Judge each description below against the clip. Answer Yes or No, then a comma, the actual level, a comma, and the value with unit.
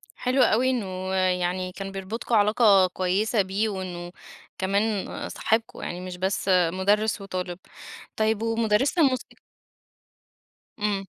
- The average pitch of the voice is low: No, high, 195 Hz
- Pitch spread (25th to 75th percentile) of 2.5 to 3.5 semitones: Yes, average, 2.9 semitones